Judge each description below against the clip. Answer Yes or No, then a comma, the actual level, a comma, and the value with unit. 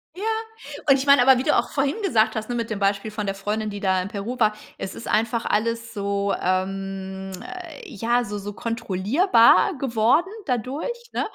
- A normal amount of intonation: Yes, average, 4.1 semitones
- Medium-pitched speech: No, high, 220 Hz